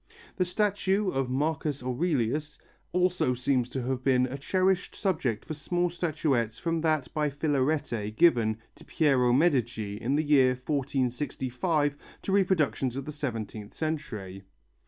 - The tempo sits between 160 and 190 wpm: No, slow, 135 wpm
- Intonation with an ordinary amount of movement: Yes, average, 4.3 semitones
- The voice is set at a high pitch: No, medium, 140 Hz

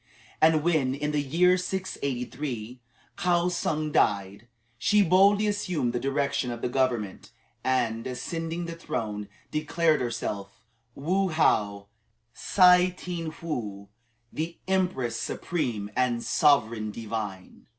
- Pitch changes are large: Yes, wide, 6.6 semitones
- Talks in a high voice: No, medium, 140 Hz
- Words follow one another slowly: Yes, slow, 115 wpm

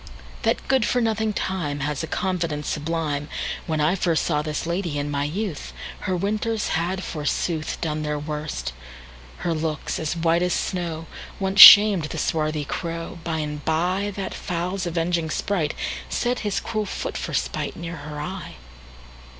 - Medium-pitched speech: Yes, medium, 165 Hz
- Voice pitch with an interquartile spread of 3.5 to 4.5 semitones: Yes, average, 3.9 semitones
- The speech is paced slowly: Yes, slow, 125 wpm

